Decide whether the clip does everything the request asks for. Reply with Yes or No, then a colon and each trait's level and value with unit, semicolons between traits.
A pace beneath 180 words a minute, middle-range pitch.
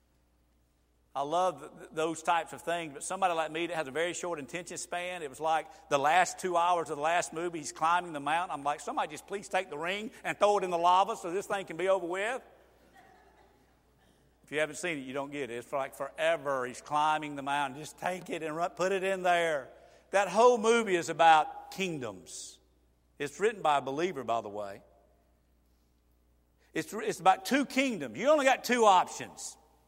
No: average, 200 wpm; medium, 165 Hz